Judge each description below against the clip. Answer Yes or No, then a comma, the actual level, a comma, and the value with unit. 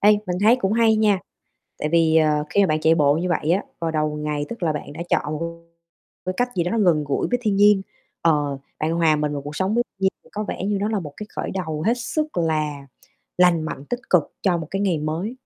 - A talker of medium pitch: Yes, medium, 170 Hz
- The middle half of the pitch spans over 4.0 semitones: Yes, average, 5.1 semitones